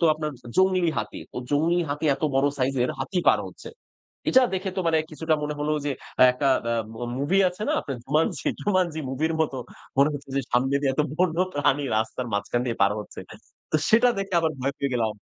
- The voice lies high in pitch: No, medium, 145 Hz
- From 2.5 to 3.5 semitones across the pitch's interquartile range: No, average, 4.2 semitones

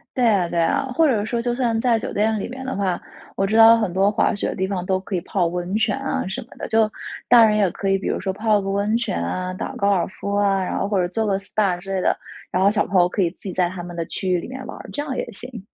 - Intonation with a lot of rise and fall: No, average, 3.2 semitones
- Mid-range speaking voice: No, high, 200 Hz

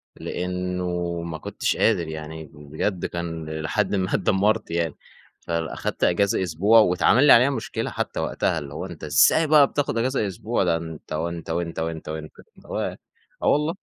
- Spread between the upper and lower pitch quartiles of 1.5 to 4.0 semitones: No, average, 4.5 semitones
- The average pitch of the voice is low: Yes, very low, 85 Hz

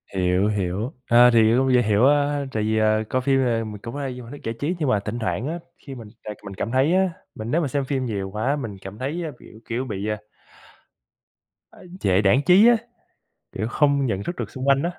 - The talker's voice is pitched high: No, low, 125 Hz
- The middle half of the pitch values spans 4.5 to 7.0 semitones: Yes, average, 4.8 semitones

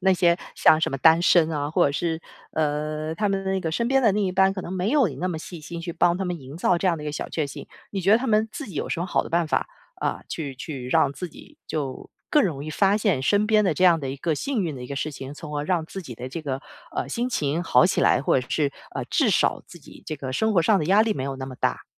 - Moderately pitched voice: Yes, medium, 165 Hz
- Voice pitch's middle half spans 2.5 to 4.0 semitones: No, average, 4.7 semitones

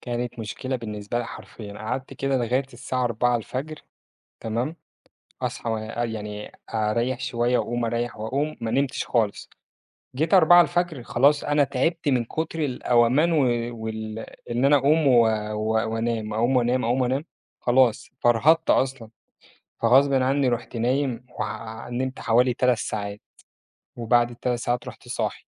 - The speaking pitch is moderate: No, low, 120 Hz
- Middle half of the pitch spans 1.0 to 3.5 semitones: Yes, average, 2.7 semitones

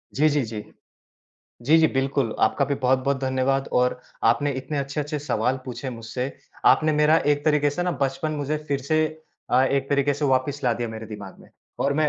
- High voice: No, medium, 140 Hz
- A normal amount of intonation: No, narrow, 2.2 semitones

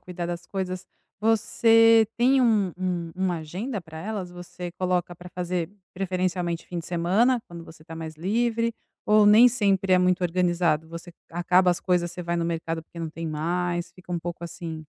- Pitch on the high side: No, medium, 180 Hz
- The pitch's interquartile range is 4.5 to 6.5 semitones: No, narrow, 2.4 semitones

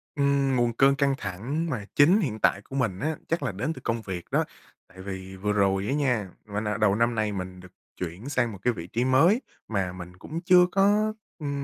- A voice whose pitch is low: Yes, low, 115 Hz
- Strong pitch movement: Yes, wide, 6.5 semitones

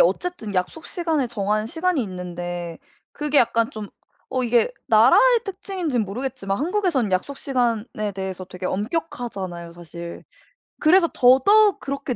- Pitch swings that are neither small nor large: No, wide, 8.9 semitones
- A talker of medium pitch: No, high, 240 Hz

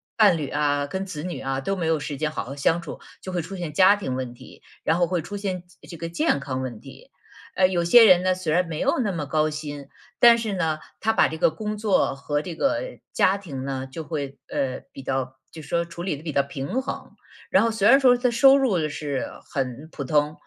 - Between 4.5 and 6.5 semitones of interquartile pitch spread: Yes, average, 4.9 semitones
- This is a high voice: No, medium, 165 Hz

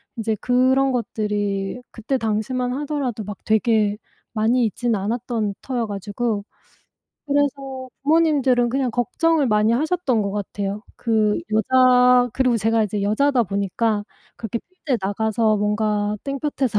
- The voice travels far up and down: No, average, 3.6 semitones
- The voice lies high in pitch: Yes, high, 230 Hz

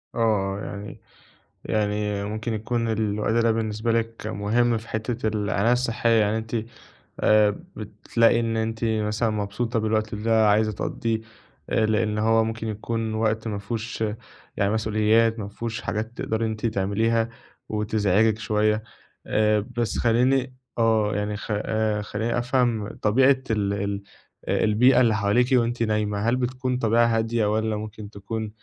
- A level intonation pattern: Yes, narrow, 1.5 semitones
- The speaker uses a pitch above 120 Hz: No, low, 110 Hz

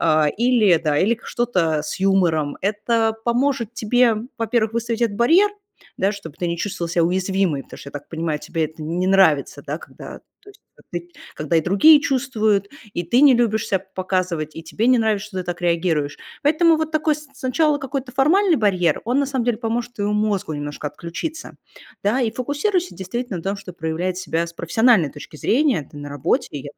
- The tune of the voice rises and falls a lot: Yes, wide, 6.4 semitones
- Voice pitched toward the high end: Yes, high, 200 Hz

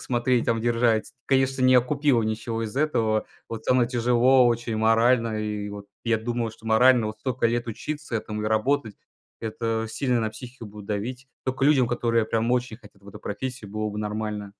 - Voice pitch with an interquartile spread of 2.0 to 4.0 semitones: Yes, narrow, 2.5 semitones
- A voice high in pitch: No, low, 115 Hz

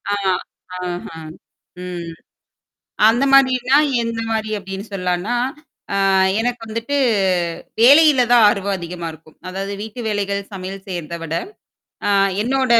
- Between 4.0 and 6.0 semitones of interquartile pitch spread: Yes, average, 4.8 semitones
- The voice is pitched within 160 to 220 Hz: Yes, high, 200 Hz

